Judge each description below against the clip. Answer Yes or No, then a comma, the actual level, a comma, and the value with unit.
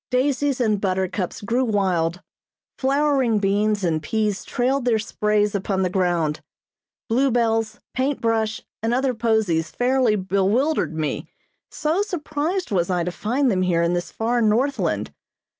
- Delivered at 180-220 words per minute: No, average, 140 wpm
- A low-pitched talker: No, high, 220 Hz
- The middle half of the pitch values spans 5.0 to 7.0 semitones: Yes, average, 5.3 semitones